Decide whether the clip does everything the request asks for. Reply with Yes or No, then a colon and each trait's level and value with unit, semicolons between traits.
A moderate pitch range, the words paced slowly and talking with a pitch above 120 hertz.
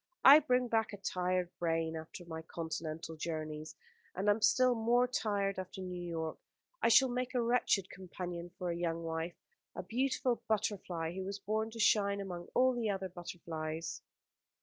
No: average, 4.9 semitones; average, 170 wpm; medium, 185 Hz